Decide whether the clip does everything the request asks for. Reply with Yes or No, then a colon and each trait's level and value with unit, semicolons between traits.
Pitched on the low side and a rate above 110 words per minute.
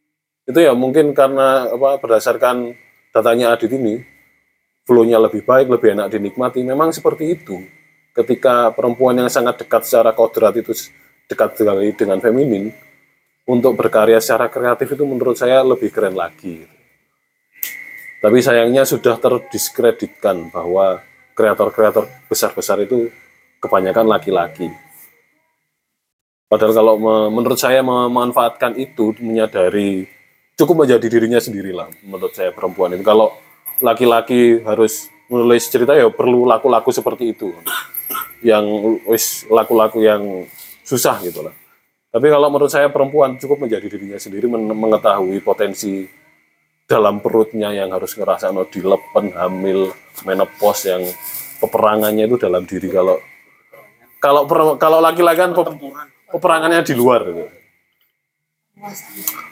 Yes: low, 120 Hz; average, 120 wpm